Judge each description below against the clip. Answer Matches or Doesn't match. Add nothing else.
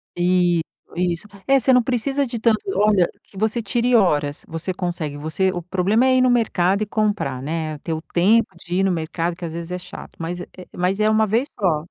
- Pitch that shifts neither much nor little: Matches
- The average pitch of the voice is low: Doesn't match